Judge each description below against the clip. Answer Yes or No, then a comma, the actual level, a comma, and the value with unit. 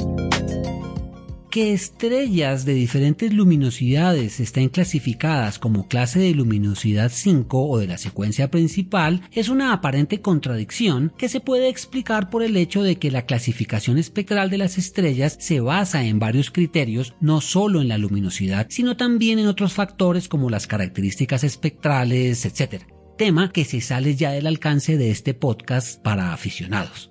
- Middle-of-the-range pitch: Yes, medium, 145 Hz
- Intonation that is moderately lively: No, wide, 7.6 semitones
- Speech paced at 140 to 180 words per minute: Yes, average, 150 wpm